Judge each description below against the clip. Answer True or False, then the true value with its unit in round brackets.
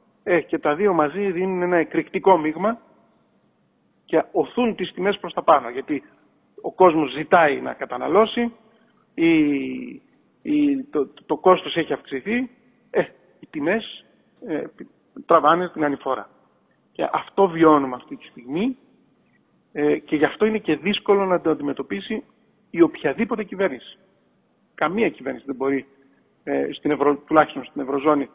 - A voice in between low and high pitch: True (180 Hz)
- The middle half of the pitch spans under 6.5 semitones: False (7.0 semitones)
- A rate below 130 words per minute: False (140 wpm)